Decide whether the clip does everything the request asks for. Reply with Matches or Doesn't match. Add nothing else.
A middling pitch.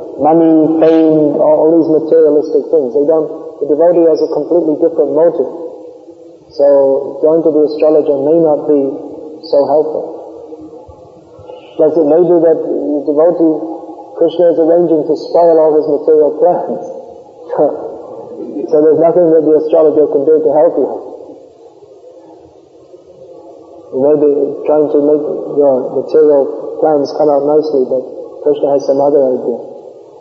Matches